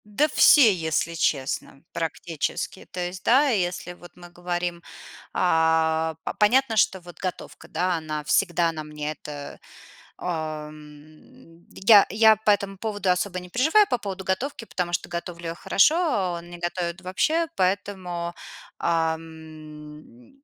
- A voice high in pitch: No, medium, 175 Hz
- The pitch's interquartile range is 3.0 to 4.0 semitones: Yes, average, 3.5 semitones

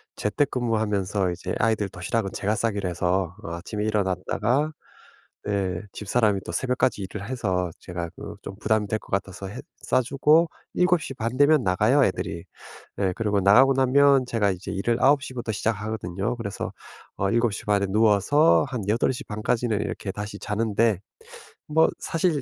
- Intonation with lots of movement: No, average, 4.3 semitones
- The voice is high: No, low, 105 Hz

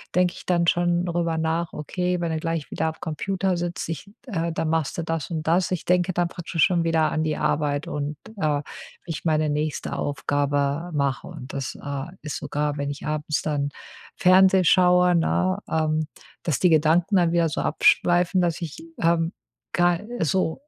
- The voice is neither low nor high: Yes, medium, 165 Hz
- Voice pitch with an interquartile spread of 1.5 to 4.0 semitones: Yes, narrow, 2.5 semitones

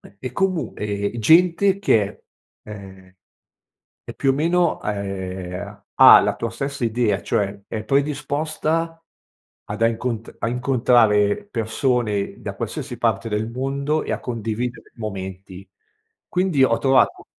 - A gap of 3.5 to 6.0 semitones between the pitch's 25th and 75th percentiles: Yes, average, 5.3 semitones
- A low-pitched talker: Yes, low, 115 Hz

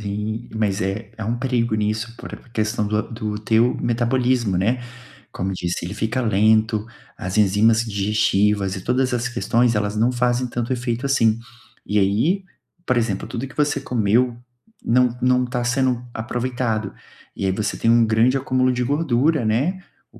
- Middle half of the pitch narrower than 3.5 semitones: Yes, average, 2.8 semitones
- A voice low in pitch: Yes, low, 115 Hz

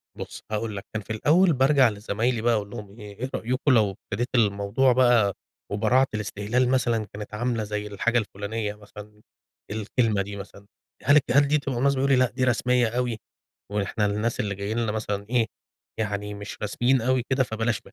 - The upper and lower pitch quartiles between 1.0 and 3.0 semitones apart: No, average, 3.4 semitones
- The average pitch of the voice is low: Yes, low, 110 Hz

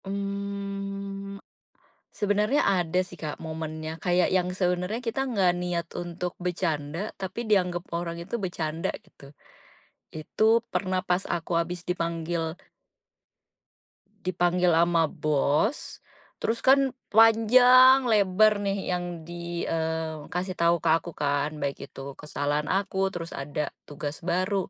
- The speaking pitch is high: No, medium, 180 Hz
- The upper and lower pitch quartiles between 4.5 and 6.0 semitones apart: No, average, 3.3 semitones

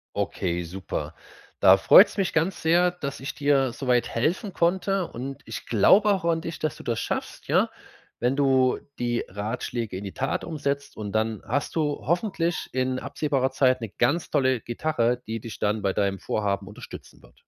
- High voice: No, low, 130 Hz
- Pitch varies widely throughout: Yes, wide, 6.3 semitones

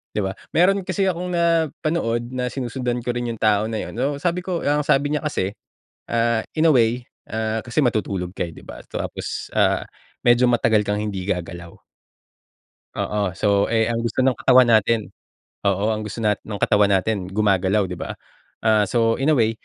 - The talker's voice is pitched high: No, low, 115 Hz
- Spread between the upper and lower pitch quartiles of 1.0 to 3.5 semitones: No, average, 3.9 semitones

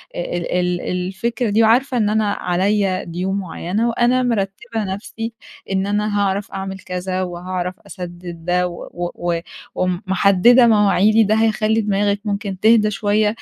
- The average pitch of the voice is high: Yes, high, 200 Hz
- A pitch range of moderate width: Yes, average, 3.0 semitones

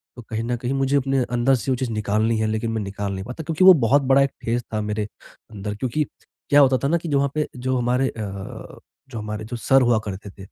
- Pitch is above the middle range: No, low, 120 Hz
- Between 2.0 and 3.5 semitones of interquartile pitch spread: No, average, 3.9 semitones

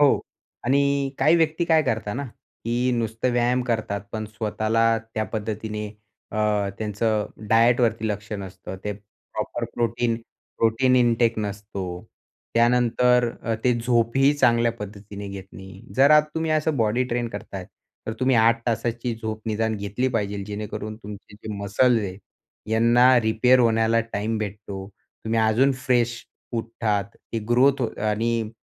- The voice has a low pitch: Yes, low, 115 Hz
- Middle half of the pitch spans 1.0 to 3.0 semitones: Yes, narrow, 2.5 semitones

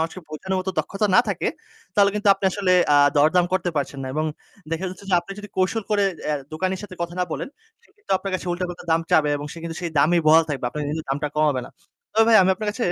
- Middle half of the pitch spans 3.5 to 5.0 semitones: Yes, average, 4.1 semitones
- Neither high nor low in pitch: Yes, medium, 180 Hz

